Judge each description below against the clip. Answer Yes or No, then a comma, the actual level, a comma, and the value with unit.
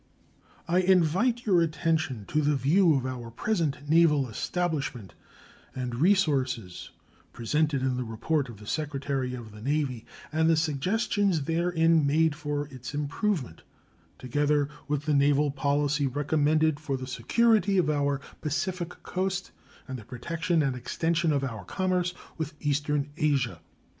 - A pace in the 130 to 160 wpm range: Yes, average, 140 wpm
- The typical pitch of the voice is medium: Yes, medium, 150 Hz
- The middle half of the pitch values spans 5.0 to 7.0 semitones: No, average, 3.7 semitones